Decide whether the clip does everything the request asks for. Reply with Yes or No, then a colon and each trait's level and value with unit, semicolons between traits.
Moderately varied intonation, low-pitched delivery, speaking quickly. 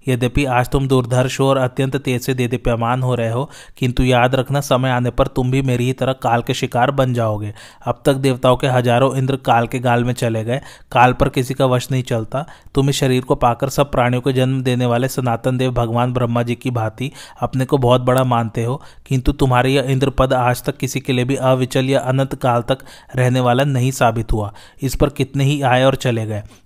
No: narrow, 1.7 semitones; low, 130 Hz; fast, 225 wpm